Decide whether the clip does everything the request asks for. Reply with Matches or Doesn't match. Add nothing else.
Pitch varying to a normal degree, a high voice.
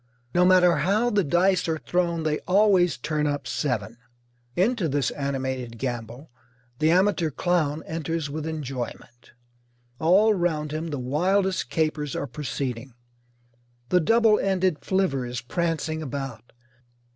Doesn't match